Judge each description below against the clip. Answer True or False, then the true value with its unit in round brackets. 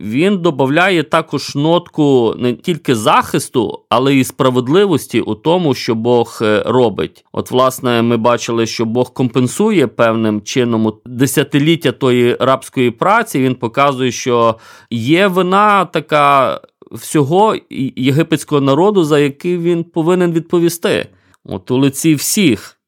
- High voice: False (135 Hz)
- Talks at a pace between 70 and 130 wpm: True (120 wpm)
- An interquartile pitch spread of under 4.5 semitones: False (5.2 semitones)